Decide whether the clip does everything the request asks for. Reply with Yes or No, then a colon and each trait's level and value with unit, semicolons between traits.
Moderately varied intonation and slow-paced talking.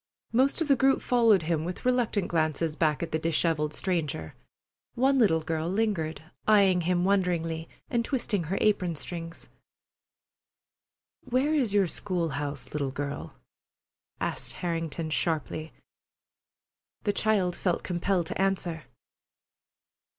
Yes: average, 4.4 semitones; slow, 125 wpm